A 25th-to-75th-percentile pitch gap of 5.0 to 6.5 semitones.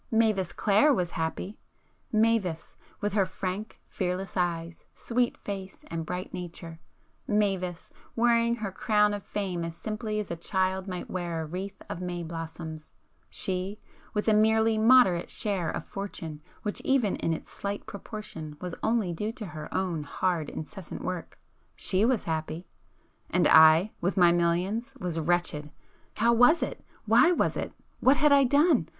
No: average, 4.1 semitones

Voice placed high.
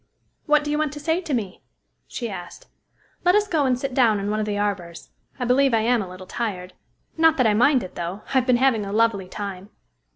Yes: high, 230 Hz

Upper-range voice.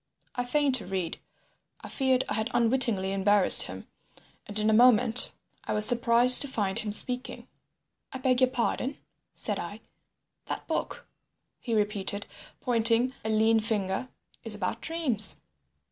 Yes: high, 225 Hz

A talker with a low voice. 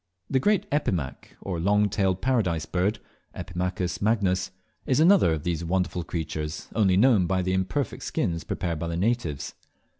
Yes: very low, 95 Hz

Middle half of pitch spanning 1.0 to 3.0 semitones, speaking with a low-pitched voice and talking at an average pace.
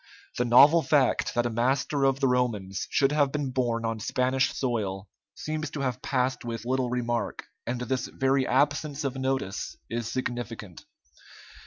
Yes: narrow, 2.4 semitones; low, 125 Hz; average, 160 wpm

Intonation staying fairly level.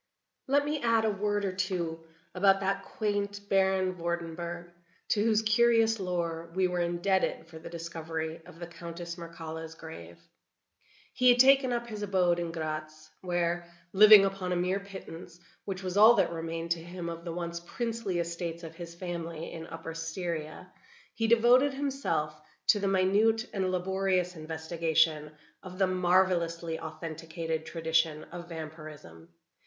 No: average, 3.1 semitones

